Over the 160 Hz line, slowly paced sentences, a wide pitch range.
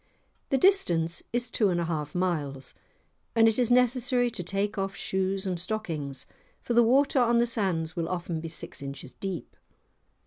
No: high, 190 Hz; average, 175 wpm; wide, 6.2 semitones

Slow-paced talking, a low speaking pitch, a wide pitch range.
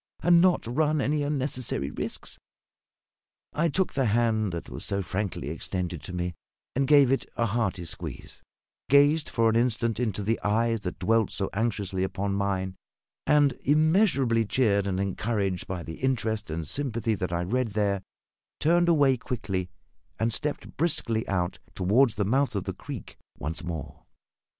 No: average, 160 wpm; low, 110 Hz; wide, 5.9 semitones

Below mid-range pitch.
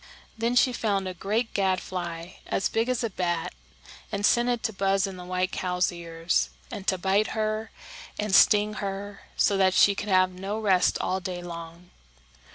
No: high, 195 Hz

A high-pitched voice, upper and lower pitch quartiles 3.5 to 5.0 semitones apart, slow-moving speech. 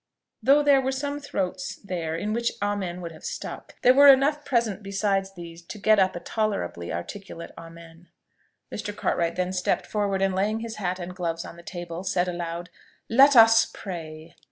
No: high, 195 Hz; average, 4.5 semitones; average, 180 wpm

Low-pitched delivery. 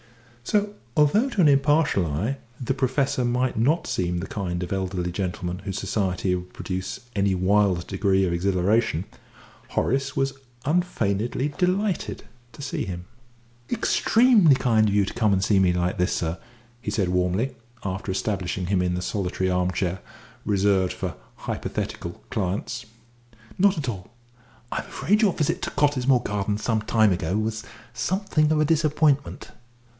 Yes: low, 105 Hz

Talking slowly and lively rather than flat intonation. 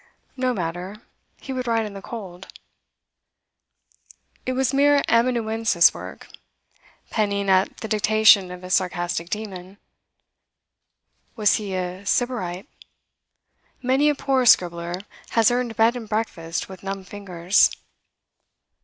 No: slow, 120 wpm; average, 4.3 semitones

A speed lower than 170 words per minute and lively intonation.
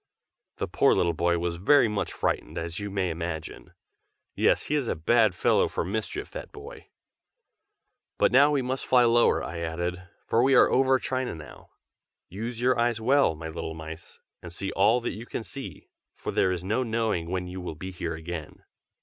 No: average, 190 wpm; wide, 6.0 semitones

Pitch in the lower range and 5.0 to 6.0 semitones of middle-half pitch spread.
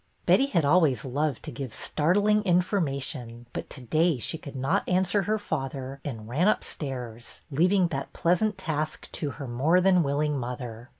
No: medium, 150 Hz; wide, 5.4 semitones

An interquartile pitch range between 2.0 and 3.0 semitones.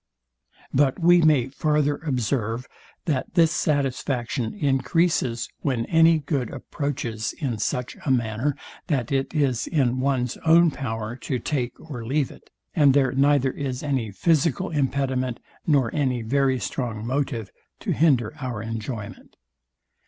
No: average, 3.4 semitones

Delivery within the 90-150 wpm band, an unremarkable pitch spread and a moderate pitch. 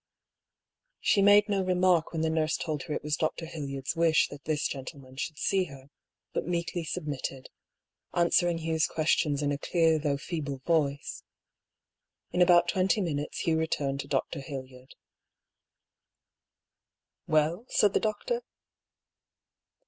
Yes: average, 145 wpm; average, 3.5 semitones; medium, 160 Hz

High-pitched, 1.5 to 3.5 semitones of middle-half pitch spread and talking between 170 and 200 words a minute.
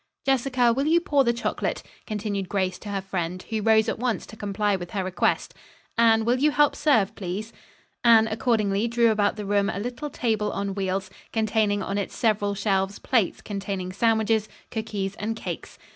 Yes: high, 215 Hz; average, 2.7 semitones; average, 180 wpm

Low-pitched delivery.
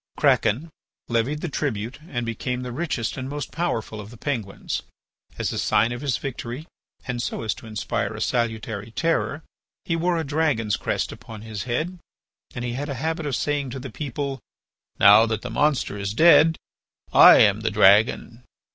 Yes: low, 125 Hz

